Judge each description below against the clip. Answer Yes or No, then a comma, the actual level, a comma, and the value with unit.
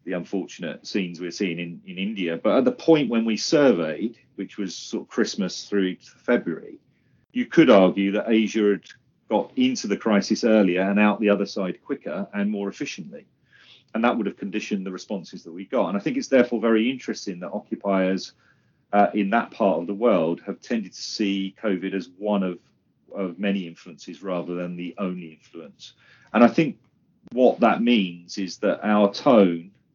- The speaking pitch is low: Yes, low, 100 Hz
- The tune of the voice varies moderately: Yes, average, 3.1 semitones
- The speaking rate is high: No, average, 190 wpm